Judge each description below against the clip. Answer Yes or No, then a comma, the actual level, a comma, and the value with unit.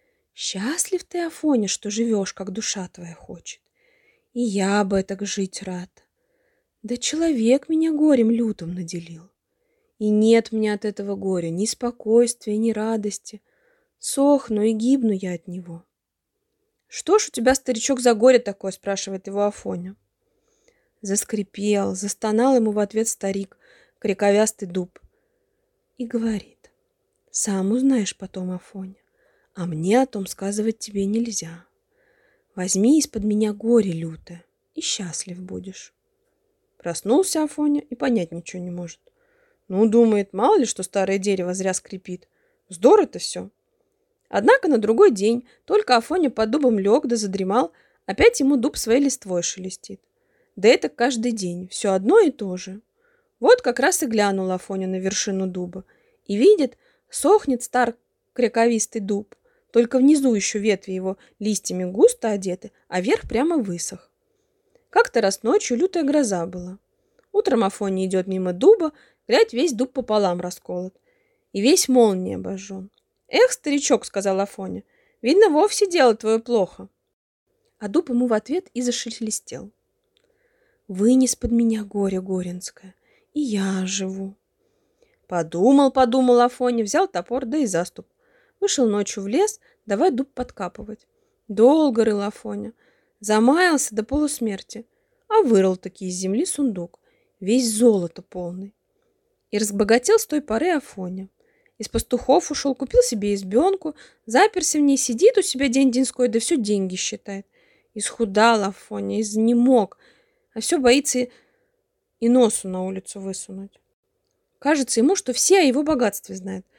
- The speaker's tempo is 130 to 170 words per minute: Yes, average, 135 wpm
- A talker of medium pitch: No, high, 235 Hz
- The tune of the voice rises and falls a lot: Yes, wide, 9.0 semitones